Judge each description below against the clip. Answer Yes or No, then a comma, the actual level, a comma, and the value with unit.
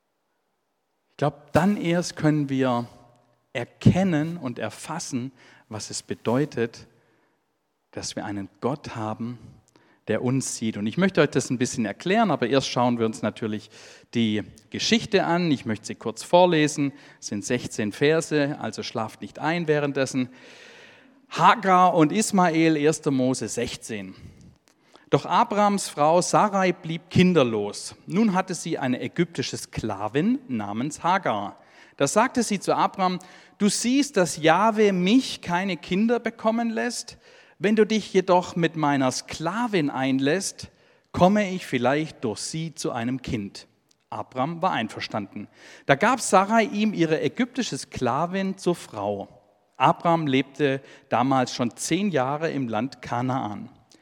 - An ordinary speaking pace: Yes, average, 135 wpm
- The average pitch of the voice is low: No, medium, 150 Hz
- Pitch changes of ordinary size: No, wide, 7.1 semitones